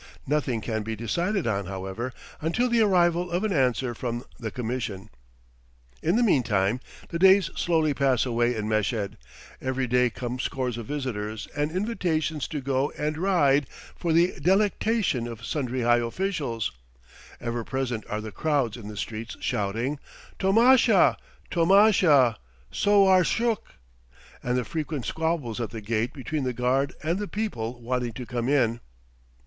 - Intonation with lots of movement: Yes, wide, 6.6 semitones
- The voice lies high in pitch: No, low, 130 Hz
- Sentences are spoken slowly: No, average, 150 wpm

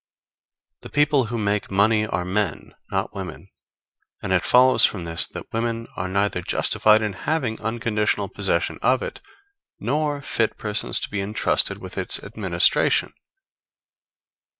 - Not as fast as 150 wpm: Yes, average, 140 wpm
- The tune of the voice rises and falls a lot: No, average, 3.2 semitones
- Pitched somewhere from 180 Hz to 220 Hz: No, low, 105 Hz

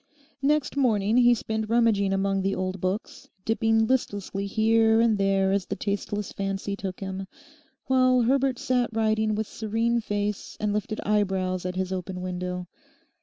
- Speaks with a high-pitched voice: Yes, high, 210 Hz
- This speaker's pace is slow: No, average, 155 wpm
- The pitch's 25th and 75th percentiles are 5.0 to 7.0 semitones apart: No, average, 2.7 semitones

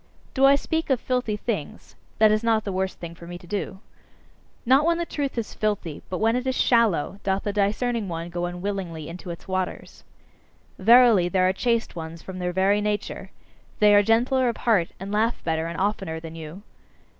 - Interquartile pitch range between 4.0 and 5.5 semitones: Yes, average, 4.8 semitones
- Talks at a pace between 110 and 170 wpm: No, average, 200 wpm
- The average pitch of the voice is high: Yes, high, 200 Hz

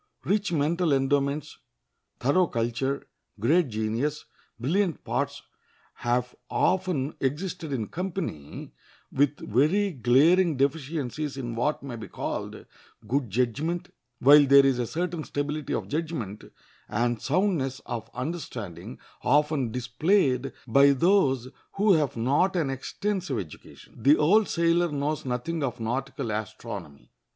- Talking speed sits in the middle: No, slow, 120 wpm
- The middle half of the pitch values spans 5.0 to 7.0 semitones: Yes, average, 5.3 semitones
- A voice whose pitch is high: No, medium, 140 Hz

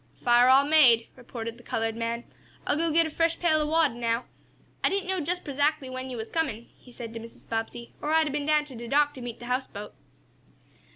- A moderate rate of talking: No, fast, 230 wpm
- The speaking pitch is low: No, very high, 260 Hz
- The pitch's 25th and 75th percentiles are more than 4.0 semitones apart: Yes, average, 4.7 semitones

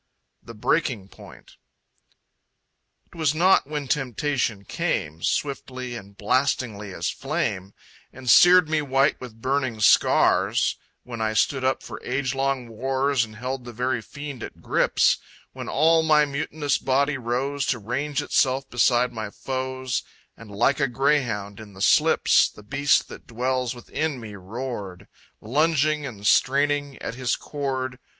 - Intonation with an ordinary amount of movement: Yes, average, 3.6 semitones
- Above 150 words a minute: No, average, 145 wpm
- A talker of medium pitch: No, low, 130 Hz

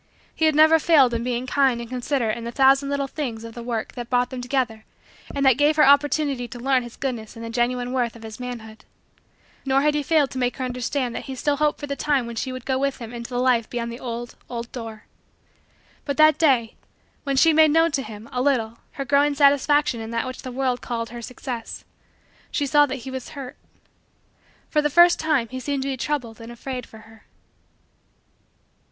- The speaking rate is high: Yes, fast, 220 wpm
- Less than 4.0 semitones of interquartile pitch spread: Yes, average, 3.1 semitones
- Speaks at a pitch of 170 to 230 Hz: No, very high, 255 Hz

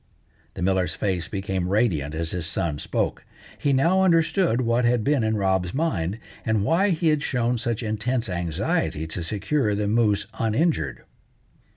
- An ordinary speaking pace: Yes, average, 160 wpm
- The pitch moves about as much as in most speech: No, wide, 6.0 semitones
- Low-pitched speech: Yes, low, 110 Hz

